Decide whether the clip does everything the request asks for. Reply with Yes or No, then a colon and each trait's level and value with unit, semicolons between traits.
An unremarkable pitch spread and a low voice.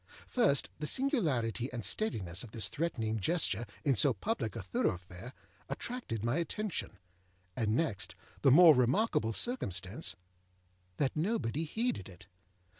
No: wide, 7.9 semitones; low, 125 Hz